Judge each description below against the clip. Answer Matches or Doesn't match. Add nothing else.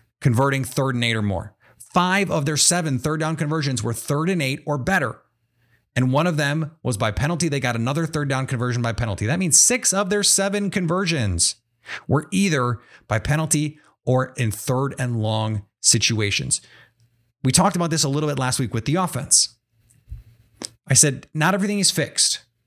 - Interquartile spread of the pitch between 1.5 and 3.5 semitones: Doesn't match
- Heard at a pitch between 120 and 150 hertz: Matches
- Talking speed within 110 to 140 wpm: Doesn't match